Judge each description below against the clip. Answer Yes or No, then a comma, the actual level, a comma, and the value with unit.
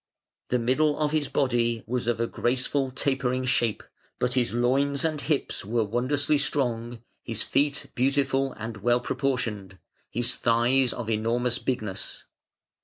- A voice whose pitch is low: Yes, low, 125 Hz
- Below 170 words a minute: Yes, average, 140 wpm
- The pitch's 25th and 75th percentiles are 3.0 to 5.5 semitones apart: No, narrow, 2.6 semitones